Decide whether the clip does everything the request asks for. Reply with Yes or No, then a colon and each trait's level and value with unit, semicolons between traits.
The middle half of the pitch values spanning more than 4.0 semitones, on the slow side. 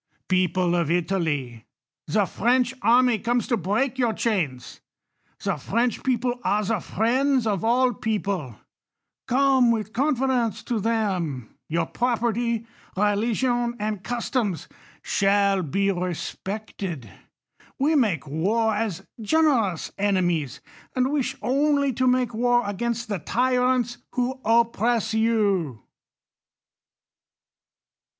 Yes: average, 4.4 semitones; slow, 115 wpm